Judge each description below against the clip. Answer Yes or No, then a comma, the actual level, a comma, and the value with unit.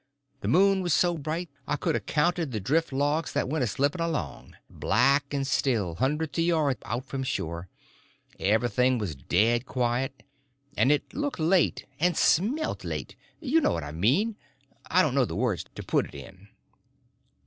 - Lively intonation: Yes, wide, 5.8 semitones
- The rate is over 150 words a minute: Yes, average, 170 wpm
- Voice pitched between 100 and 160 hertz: Yes, low, 135 Hz